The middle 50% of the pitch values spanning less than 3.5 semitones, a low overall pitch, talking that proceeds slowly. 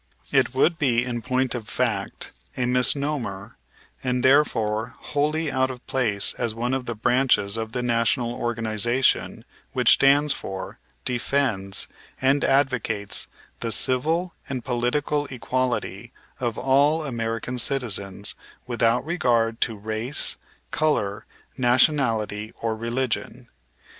Yes: average, 2.8 semitones; low, 125 Hz; slow, 120 wpm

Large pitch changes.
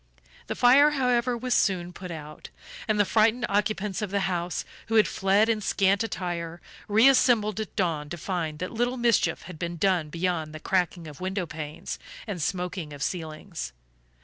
No: average, 4.4 semitones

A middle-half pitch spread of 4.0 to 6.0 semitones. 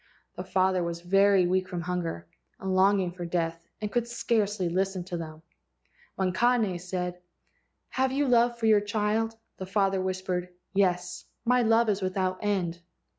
No: average, 2.8 semitones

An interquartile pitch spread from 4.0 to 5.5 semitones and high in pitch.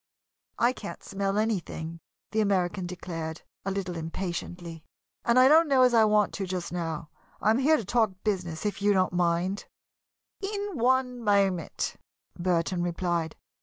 Yes: average, 4.4 semitones; high, 195 Hz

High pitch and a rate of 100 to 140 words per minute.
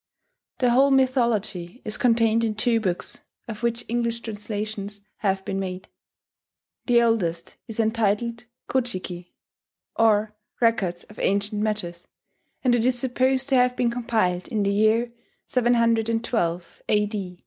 Yes: high, 225 Hz; slow, 135 wpm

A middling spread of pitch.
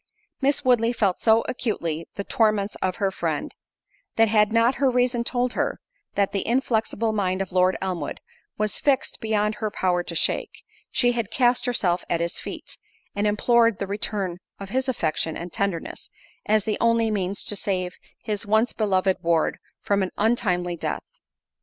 Yes: average, 3.6 semitones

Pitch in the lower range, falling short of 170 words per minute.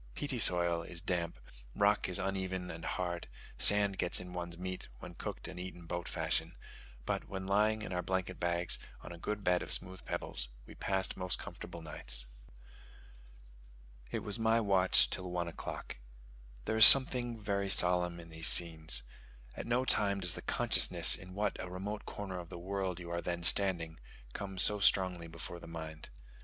No: very low, 90 Hz; average, 175 wpm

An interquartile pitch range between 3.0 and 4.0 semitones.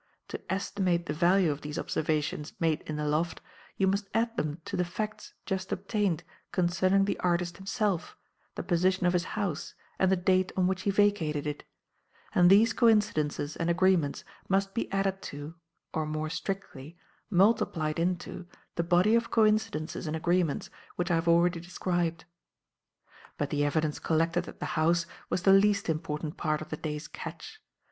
Yes: average, 3.6 semitones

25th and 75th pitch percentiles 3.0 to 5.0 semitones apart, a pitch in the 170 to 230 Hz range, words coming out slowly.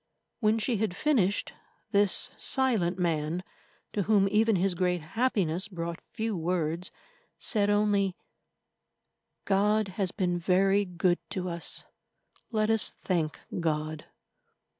Yes: average, 3.4 semitones; high, 190 Hz; slow, 120 wpm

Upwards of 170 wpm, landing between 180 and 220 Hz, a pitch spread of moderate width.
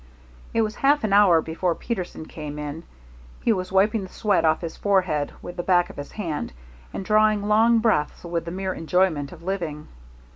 Yes: average, 190 wpm; medium, 185 Hz; average, 4.5 semitones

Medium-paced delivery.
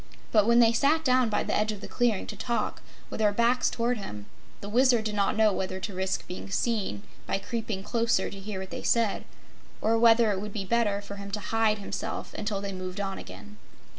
No: fast, 225 wpm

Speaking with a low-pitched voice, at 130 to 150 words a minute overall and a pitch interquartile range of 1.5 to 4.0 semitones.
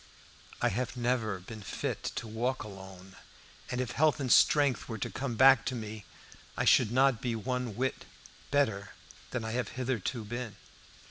No: low, 120 Hz; average, 165 wpm; average, 2.9 semitones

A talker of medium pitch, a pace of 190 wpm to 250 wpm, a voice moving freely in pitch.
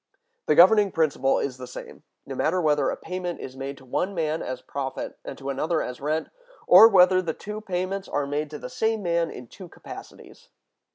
No: medium, 160 Hz; fast, 205 wpm; average, 5.0 semitones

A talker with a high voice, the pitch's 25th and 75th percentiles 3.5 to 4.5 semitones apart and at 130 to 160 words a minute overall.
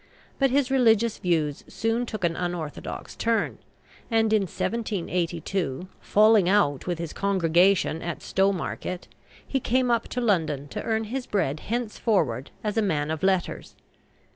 No: high, 195 Hz; average, 5.1 semitones; average, 140 wpm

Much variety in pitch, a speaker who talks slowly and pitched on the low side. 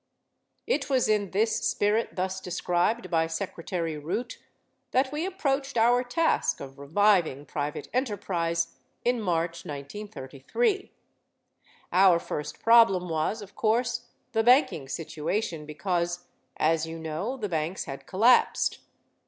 No: wide, 6.2 semitones; slow, 120 wpm; high, 190 Hz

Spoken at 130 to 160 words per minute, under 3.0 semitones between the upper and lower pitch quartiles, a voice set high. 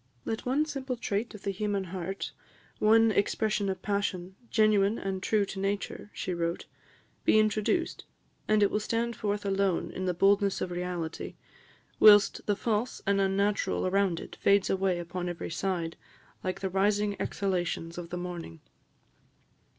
Yes: average, 155 wpm; narrow, 2.4 semitones; high, 195 Hz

